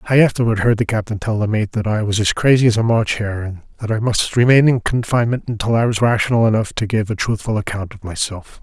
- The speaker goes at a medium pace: No, fast, 250 wpm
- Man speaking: Yes, male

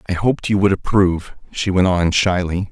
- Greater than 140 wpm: Yes, average, 200 wpm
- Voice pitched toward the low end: Yes, very low, 95 Hz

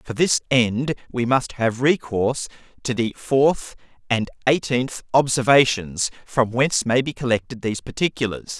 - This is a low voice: Yes, low, 125 Hz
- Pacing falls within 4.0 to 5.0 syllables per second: Yes, 4.8 syllables/s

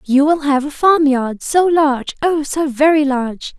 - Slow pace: No, average, 200 wpm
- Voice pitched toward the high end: Yes, very high, 290 Hz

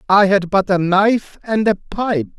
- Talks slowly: No, average, 200 wpm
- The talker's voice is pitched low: No, high, 200 Hz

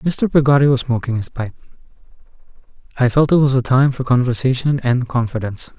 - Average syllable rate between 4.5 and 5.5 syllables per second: No, 5.9 syllables/s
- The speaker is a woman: No, male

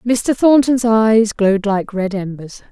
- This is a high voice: Yes, high, 215 Hz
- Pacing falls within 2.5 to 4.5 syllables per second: Yes, 4.0 syllables/s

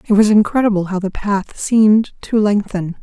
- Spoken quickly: No, average, 180 wpm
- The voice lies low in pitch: No, high, 205 Hz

